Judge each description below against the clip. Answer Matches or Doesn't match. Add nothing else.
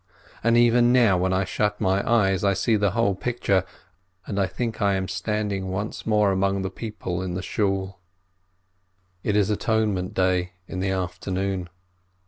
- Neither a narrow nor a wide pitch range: Doesn't match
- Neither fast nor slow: Matches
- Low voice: Matches